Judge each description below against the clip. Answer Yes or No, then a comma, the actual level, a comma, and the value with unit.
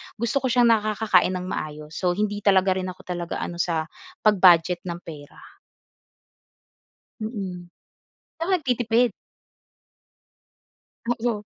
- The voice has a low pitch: No, high, 195 Hz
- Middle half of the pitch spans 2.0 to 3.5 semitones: No, average, 4.3 semitones